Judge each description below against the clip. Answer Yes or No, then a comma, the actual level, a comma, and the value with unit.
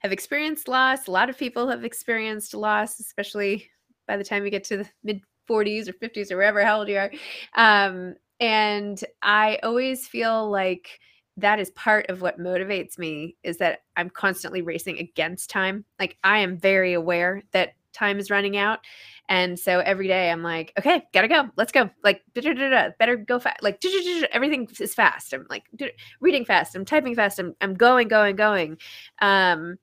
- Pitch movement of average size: Yes, average, 3.3 semitones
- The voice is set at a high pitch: Yes, high, 205 Hz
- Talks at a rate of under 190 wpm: Yes, average, 175 wpm